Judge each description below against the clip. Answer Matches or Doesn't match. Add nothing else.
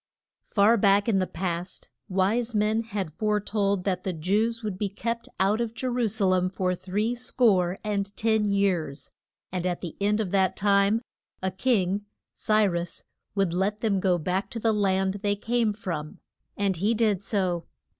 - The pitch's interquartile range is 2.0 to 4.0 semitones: Matches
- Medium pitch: Doesn't match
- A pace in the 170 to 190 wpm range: Matches